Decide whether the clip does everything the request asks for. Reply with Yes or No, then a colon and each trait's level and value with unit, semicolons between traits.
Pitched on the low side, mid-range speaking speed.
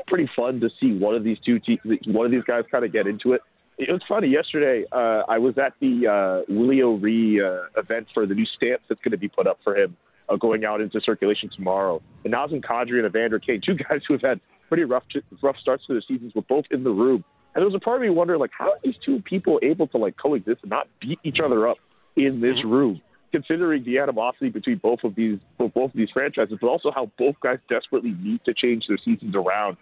No: low, 125 Hz; fast, 245 wpm